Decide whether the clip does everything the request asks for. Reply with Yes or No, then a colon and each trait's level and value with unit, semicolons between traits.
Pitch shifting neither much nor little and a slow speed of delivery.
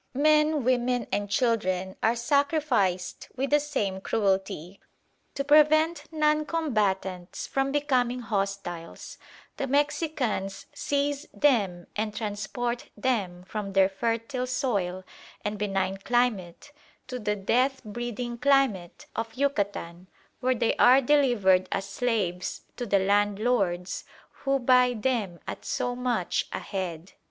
No: wide, 5.7 semitones; slow, 120 wpm